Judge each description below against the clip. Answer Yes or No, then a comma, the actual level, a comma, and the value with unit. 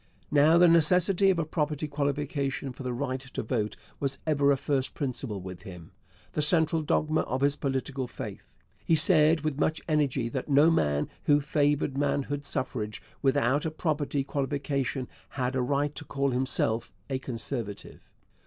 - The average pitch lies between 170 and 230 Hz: No, medium, 140 Hz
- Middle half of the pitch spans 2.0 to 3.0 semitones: Yes, average, 2.7 semitones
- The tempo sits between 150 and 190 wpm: Yes, average, 160 wpm